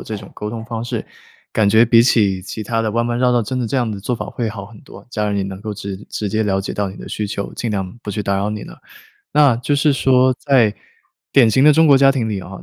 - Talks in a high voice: No, low, 110 Hz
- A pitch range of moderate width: Yes, average, 3.4 semitones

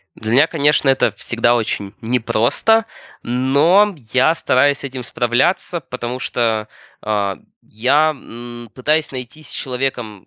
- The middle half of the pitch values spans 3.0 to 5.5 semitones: Yes, average, 3.8 semitones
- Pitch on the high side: No, low, 125 Hz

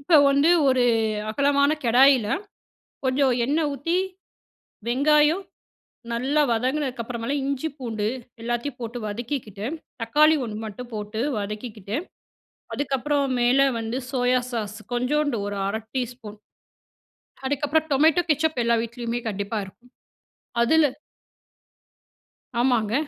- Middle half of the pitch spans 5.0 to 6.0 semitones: No, average, 3.8 semitones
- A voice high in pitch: Yes, very high, 250 Hz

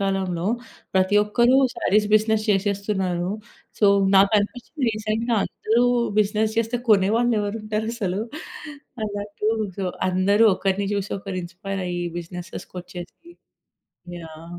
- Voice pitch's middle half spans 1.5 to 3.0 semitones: Yes, narrow, 2.5 semitones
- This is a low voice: No, high, 205 Hz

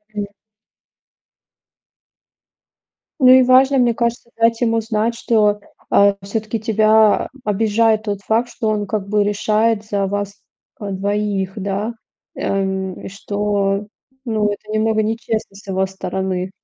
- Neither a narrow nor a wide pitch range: No, narrow, 2.0 semitones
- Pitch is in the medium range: No, high, 210 Hz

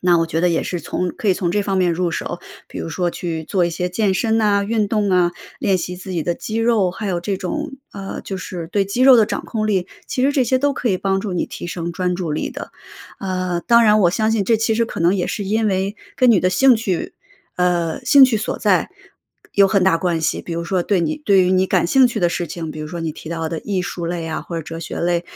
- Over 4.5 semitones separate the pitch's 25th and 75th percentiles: No, average, 3.7 semitones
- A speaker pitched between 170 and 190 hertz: Yes, medium, 185 Hz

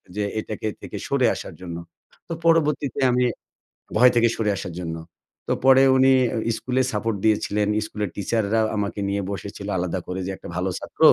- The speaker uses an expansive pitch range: No, average, 3.8 semitones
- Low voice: Yes, low, 105 Hz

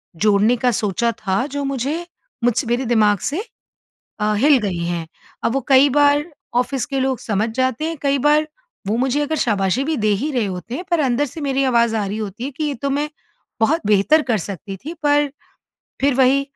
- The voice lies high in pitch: Yes, very high, 260 Hz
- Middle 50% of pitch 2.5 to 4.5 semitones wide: No, average, 5.1 semitones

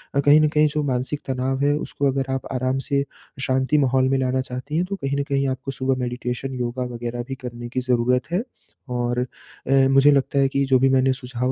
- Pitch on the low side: Yes, low, 130 Hz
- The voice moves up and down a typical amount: No, narrow, 1.6 semitones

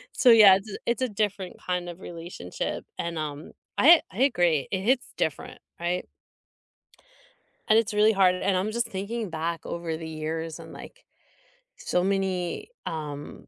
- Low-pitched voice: No, medium, 185 Hz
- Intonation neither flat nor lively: Yes, average, 4.3 semitones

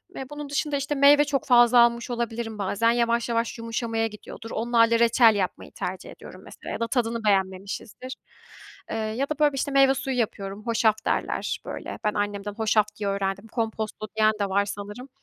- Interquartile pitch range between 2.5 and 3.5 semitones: Yes, average, 3.1 semitones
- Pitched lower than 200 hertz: No, high, 230 Hz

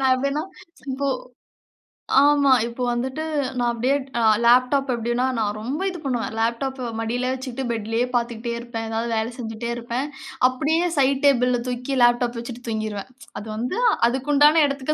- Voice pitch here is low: No, high, 245 Hz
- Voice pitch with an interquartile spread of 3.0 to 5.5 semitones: No, narrow, 2.4 semitones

